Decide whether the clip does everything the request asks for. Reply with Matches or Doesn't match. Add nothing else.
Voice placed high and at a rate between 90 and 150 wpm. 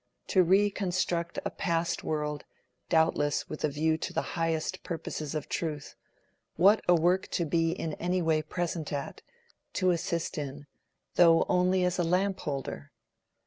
Doesn't match